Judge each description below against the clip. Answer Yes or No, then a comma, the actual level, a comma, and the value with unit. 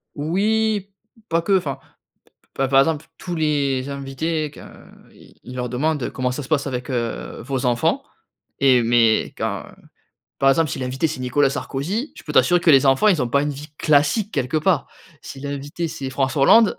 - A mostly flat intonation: No, average, 3.5 semitones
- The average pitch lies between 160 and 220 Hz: No, medium, 140 Hz